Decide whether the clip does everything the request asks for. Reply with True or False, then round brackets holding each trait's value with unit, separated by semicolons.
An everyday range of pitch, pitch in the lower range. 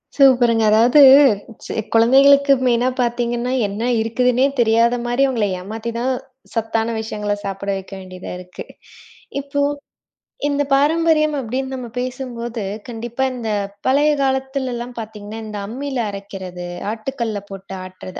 False (3.7 semitones; 235 Hz)